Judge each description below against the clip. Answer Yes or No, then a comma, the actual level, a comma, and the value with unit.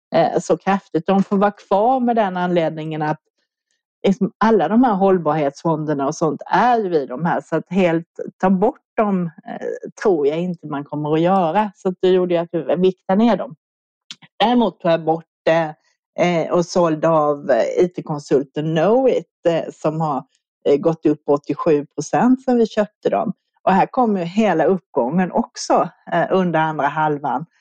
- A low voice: No, medium, 175 Hz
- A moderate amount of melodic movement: Yes, average, 4.6 semitones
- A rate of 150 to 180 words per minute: Yes, average, 165 wpm